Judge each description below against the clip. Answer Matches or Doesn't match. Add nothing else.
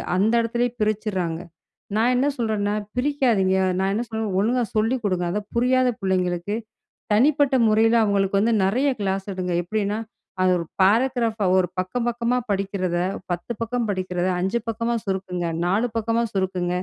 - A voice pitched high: Matches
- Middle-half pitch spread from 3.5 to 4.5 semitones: Matches